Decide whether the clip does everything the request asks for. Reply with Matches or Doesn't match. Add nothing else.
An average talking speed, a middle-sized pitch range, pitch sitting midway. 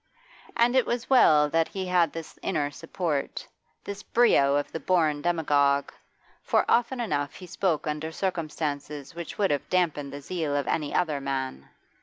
Matches